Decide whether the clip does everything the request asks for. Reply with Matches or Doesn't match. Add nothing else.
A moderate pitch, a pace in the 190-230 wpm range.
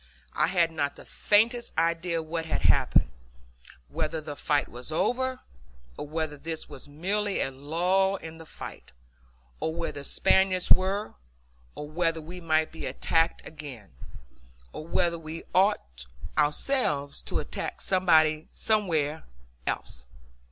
Doesn't match